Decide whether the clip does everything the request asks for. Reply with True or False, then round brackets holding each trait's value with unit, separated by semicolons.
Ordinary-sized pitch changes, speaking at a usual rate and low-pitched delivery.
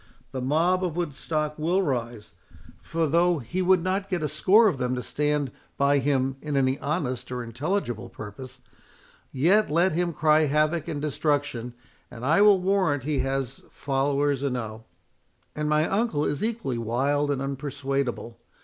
False (4.0 semitones; 160 wpm; 145 Hz)